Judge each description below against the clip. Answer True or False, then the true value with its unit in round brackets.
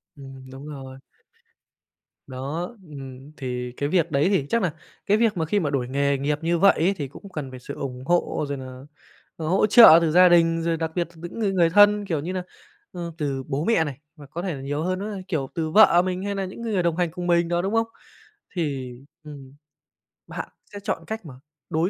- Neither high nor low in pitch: True (165 Hz)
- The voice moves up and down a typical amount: True (4.7 semitones)